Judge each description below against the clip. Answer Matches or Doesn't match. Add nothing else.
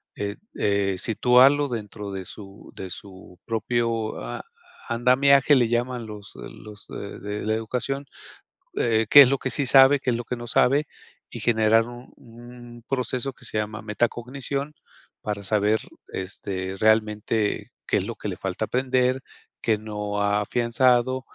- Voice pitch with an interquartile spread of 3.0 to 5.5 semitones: Matches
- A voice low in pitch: Matches